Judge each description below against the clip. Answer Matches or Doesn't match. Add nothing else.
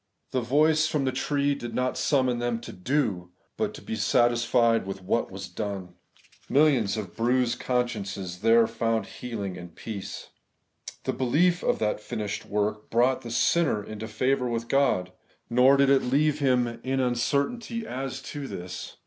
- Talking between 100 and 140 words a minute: Doesn't match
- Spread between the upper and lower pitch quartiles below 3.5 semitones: Doesn't match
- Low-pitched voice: Matches